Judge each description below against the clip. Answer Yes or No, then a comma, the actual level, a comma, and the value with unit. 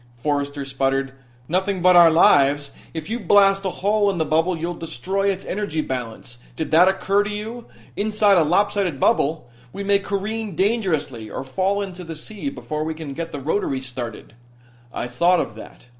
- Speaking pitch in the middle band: Yes, medium, 170 Hz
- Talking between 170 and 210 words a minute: Yes, average, 180 wpm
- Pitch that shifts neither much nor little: No, wide, 5.8 semitones